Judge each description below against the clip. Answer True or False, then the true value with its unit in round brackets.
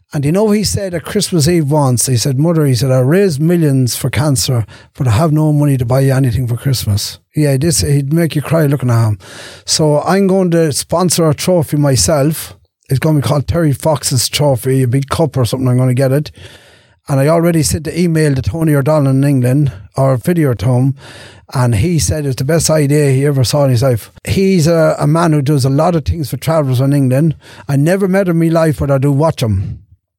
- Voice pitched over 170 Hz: False (140 Hz)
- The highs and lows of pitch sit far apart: False (3.7 semitones)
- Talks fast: True (235 wpm)